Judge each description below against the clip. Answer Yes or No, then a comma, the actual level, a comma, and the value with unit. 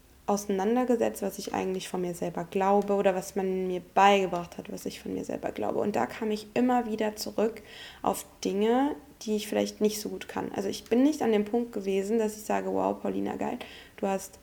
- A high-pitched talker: Yes, high, 205 Hz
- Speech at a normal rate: No, fast, 215 wpm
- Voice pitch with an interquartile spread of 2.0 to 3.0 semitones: Yes, narrow, 2.6 semitones